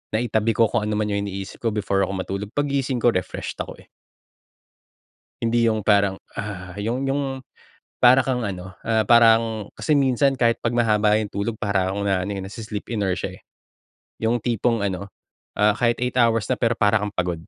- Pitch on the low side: Yes, low, 110 Hz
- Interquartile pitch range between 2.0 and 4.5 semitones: Yes, average, 2.8 semitones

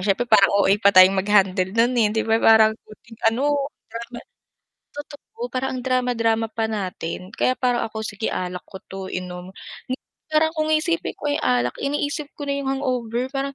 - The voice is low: No, high, 230 Hz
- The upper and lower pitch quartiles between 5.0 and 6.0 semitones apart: Yes, wide, 5.5 semitones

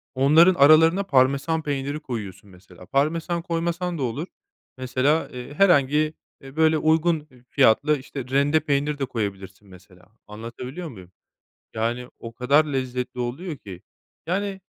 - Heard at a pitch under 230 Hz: Yes, medium, 140 Hz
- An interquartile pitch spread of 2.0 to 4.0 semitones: No, average, 4.7 semitones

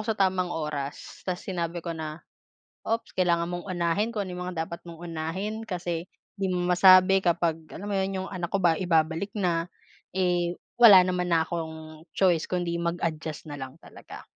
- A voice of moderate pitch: Yes, medium, 175 Hz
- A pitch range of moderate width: No, narrow, 2.2 semitones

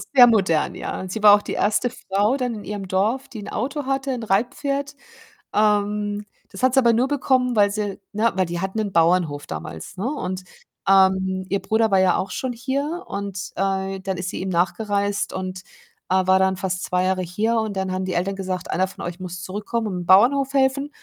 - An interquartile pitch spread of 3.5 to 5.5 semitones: Yes, average, 3.8 semitones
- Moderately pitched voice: No, high, 200 Hz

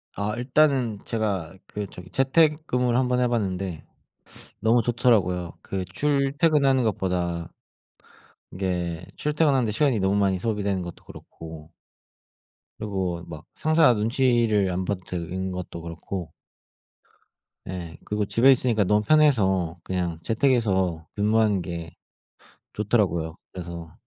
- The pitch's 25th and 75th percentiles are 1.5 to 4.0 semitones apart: No, wide, 5.4 semitones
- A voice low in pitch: Yes, low, 100 Hz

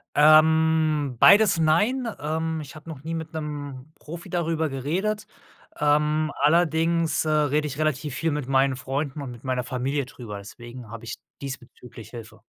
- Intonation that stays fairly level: No, average, 3.2 semitones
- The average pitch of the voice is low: No, medium, 150 Hz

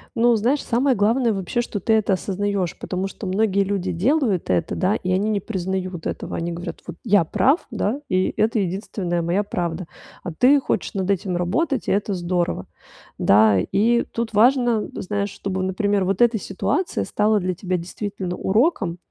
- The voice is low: No, high, 200 Hz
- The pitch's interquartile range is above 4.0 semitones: No, average, 3.5 semitones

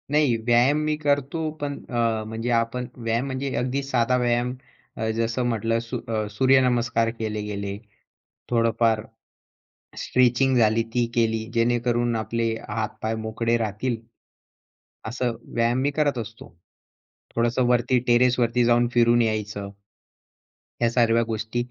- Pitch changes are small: Yes, narrow, 1.7 semitones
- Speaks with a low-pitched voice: Yes, low, 120 Hz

